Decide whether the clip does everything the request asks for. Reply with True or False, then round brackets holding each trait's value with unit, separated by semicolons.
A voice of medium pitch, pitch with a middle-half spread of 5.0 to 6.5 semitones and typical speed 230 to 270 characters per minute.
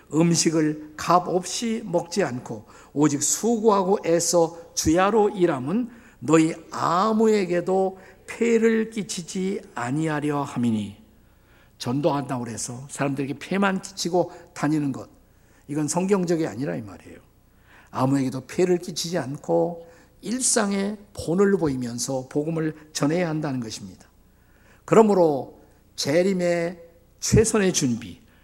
True (165 Hz; 5.4 semitones; 260 characters per minute)